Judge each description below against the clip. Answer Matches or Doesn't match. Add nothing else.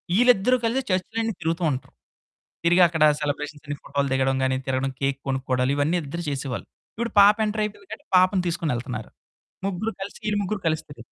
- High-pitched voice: Doesn't match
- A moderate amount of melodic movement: Doesn't match